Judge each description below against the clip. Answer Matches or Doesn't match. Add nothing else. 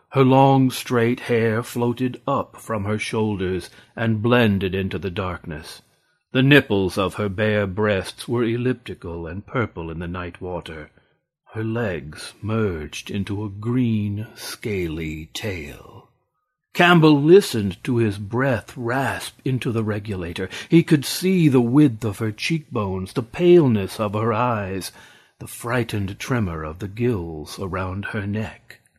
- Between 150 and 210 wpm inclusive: Doesn't match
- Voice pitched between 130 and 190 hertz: Doesn't match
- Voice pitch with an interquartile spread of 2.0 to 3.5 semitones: Doesn't match